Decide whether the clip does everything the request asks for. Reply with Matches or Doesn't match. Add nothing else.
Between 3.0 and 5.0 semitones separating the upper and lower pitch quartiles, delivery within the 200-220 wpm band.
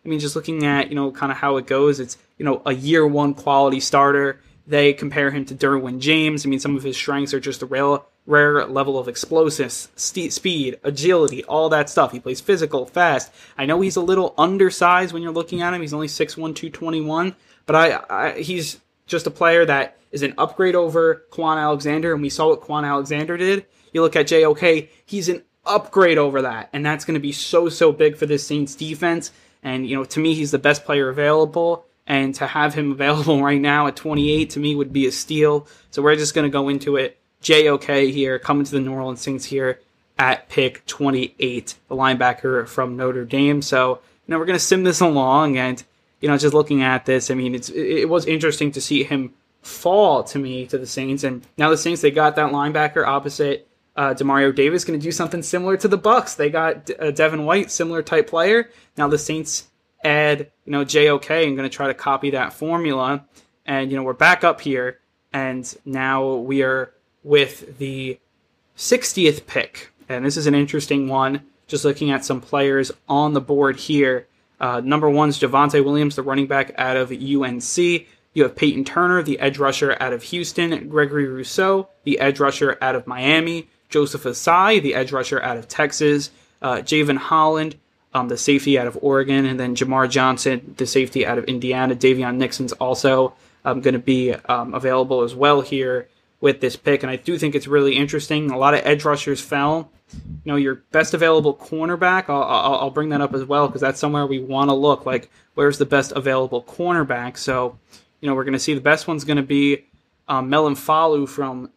Doesn't match